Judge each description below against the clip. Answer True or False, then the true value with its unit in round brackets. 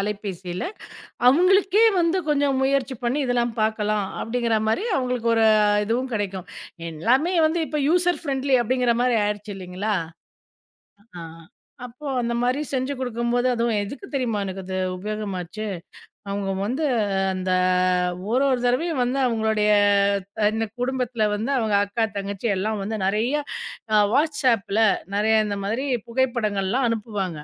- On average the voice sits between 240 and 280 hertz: False (230 Hz)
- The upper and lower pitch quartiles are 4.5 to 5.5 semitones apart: False (3.9 semitones)